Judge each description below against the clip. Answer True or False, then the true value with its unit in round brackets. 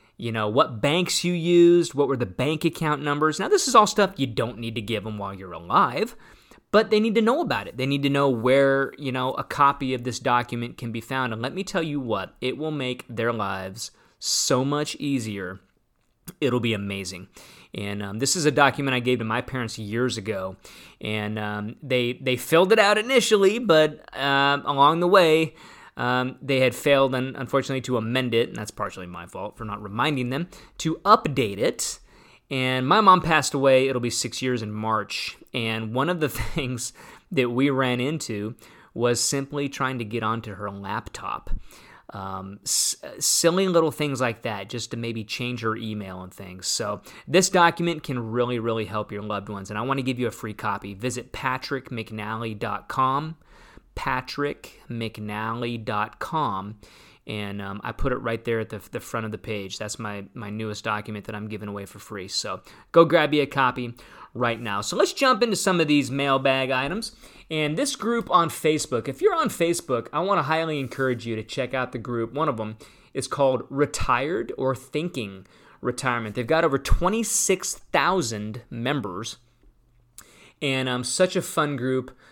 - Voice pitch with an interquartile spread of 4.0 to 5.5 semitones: True (4.8 semitones)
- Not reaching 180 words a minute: False (190 wpm)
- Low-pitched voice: True (125 Hz)